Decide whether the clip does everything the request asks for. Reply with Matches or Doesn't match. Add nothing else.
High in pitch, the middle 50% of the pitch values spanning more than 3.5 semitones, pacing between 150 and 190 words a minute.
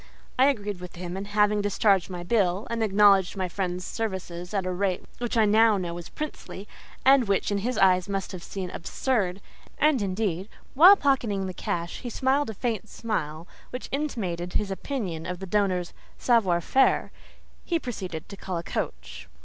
Matches